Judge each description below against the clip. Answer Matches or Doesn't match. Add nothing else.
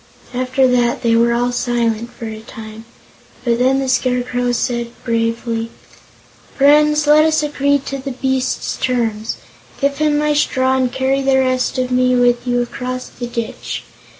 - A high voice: Matches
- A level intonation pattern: Matches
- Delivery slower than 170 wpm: Matches